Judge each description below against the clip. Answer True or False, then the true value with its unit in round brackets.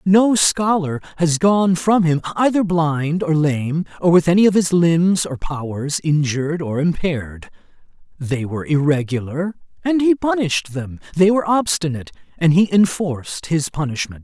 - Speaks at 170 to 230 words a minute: False (150 wpm)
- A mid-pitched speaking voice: True (165 Hz)